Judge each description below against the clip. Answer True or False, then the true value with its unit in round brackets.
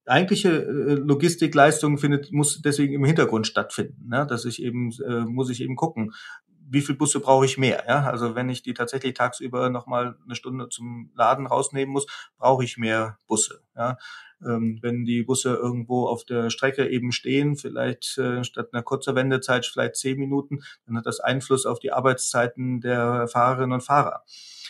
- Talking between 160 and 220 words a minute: True (175 wpm)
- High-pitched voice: False (125 Hz)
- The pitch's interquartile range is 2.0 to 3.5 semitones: True (2.6 semitones)